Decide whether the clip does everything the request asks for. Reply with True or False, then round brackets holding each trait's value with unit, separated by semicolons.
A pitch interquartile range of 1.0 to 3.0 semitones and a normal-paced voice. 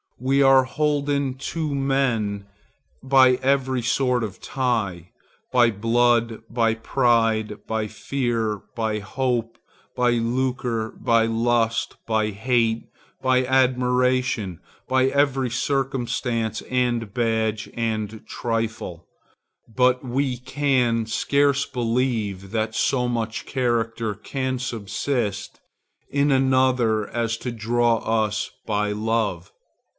False (2.7 semitones; 100 wpm)